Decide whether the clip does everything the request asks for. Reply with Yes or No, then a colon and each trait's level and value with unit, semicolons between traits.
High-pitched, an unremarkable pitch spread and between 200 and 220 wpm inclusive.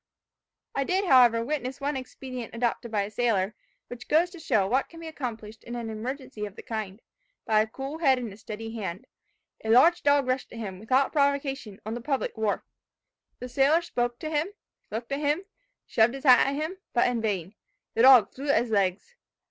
Yes: high, 245 Hz; average, 4.2 semitones; fast, 205 wpm